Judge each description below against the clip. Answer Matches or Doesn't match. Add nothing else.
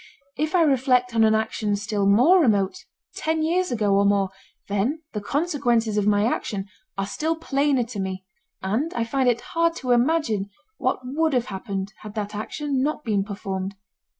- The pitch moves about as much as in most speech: Doesn't match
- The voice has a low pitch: Doesn't match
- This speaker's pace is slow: Doesn't match